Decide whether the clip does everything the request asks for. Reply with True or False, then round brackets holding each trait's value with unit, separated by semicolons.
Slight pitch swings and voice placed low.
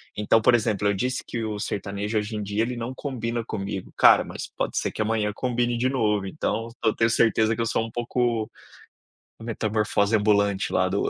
True (2.0 semitones; 110 Hz)